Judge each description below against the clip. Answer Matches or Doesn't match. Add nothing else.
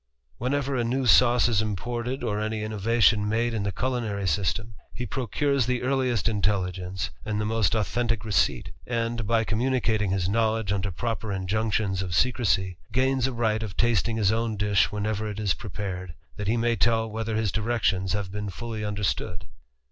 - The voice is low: Matches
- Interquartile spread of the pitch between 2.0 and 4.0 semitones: Matches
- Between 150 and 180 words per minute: Matches